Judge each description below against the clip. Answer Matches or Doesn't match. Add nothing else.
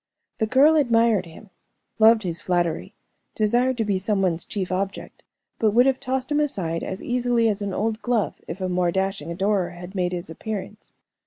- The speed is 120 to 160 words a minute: Doesn't match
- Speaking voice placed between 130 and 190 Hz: Doesn't match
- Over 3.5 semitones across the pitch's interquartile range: Matches